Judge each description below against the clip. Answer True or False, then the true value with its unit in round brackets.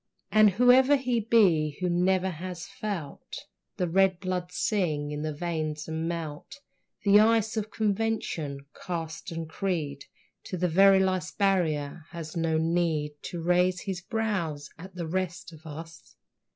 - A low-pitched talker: False (175 Hz)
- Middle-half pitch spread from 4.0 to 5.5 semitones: False (3.6 semitones)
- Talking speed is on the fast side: False (150 wpm)